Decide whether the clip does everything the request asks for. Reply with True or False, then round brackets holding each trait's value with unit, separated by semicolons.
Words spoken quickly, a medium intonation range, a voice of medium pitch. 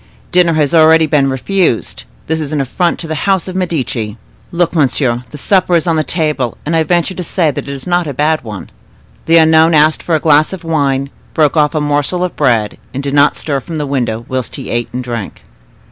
True (225 wpm; 3.4 semitones; 155 Hz)